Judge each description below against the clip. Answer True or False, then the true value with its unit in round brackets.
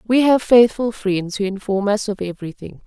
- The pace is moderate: True (190 wpm)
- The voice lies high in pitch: True (210 Hz)